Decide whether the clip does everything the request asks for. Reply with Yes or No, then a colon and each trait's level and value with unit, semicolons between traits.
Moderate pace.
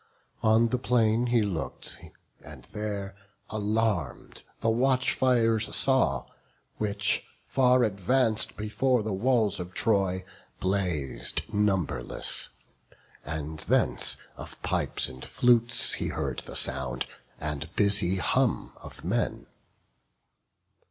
No: slow, 105 wpm